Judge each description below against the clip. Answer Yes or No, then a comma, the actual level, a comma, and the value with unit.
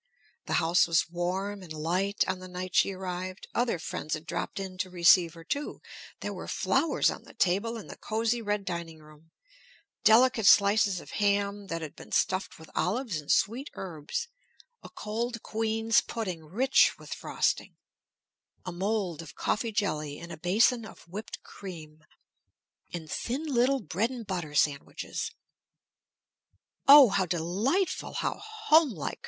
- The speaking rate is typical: Yes, average, 155 wpm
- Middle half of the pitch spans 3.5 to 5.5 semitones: Yes, average, 4.8 semitones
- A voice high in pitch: Yes, high, 195 Hz